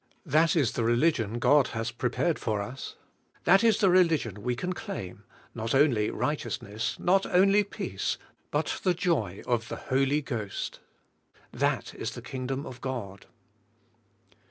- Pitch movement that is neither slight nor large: No, wide, 6.7 semitones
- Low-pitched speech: Yes, low, 130 Hz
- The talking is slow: No, average, 145 wpm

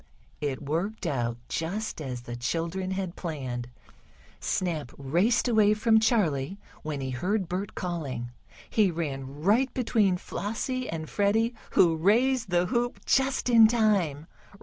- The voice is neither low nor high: Yes, medium, 180 Hz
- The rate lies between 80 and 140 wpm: Yes, slow, 135 wpm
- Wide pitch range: Yes, wide, 6.9 semitones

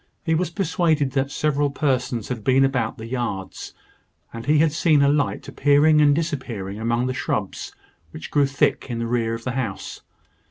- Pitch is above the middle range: No, low, 135 Hz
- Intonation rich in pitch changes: No, average, 4.2 semitones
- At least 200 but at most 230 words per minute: No, average, 185 wpm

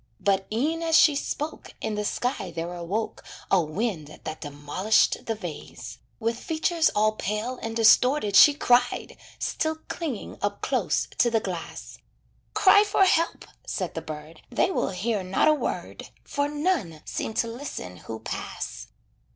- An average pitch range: No, wide, 8.5 semitones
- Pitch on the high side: Yes, high, 220 Hz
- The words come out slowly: No, average, 155 wpm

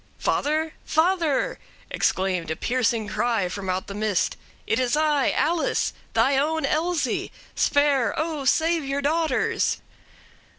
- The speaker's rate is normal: No, slow, 125 wpm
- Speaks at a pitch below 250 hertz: No, very high, 280 Hz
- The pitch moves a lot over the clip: Yes, wide, 6.1 semitones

